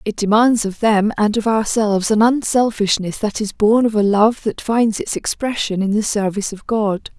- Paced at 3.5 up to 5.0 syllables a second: Yes, 4.9 syllables/s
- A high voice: Yes, high, 215 Hz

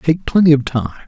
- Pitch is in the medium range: Yes, medium, 145 Hz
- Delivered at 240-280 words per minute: No, fast, 225 wpm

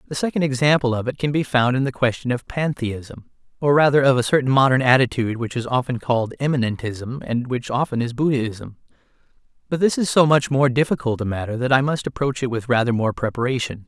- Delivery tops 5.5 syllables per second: Yes, 6.0 syllables/s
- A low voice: Yes, low, 130 Hz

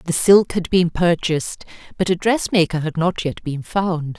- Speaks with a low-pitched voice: No, medium, 170 Hz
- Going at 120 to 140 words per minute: No, average, 200 wpm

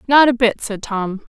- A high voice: Yes, high, 230 Hz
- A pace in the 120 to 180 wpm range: No, fast, 225 wpm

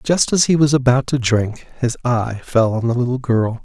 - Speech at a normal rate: No, fast, 230 wpm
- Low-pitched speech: Yes, low, 125 Hz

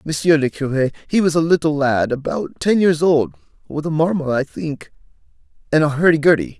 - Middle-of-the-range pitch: Yes, medium, 145 Hz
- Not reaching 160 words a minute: No, average, 190 wpm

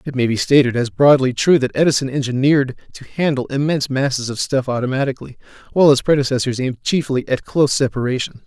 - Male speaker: Yes, male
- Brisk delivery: No, average, 175 wpm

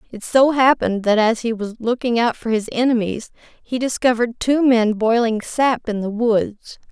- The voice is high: Yes, high, 230 Hz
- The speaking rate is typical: Yes, average, 180 wpm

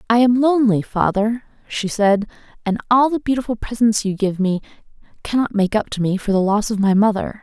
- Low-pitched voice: No, high, 215 Hz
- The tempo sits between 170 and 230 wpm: Yes, average, 200 wpm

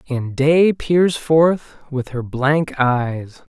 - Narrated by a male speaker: Yes, male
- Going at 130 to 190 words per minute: Yes, slow, 135 wpm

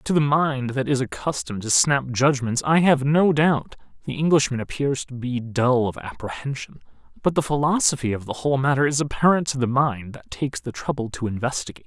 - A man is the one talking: Yes, male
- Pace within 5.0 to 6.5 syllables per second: Yes, 5.6 syllables/s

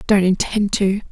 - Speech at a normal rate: Yes, average, 160 wpm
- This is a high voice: Yes, high, 200 Hz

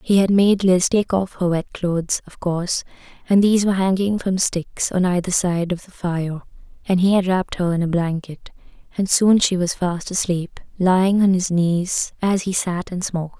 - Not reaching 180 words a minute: No, fast, 205 wpm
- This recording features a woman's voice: Yes, female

